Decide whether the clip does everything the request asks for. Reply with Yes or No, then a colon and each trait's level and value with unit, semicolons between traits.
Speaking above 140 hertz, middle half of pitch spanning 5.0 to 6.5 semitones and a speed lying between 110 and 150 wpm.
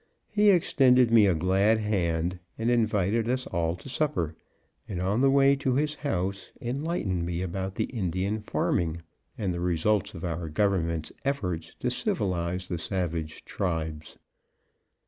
No: very low, 95 Hz; wide, 5.6 semitones; average, 145 wpm